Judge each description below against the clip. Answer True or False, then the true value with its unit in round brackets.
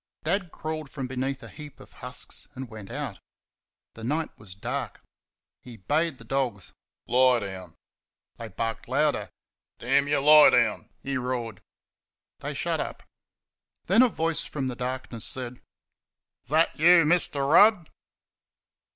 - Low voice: True (130 Hz)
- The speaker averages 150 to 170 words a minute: False (140 wpm)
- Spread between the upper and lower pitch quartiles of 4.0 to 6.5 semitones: True (4.6 semitones)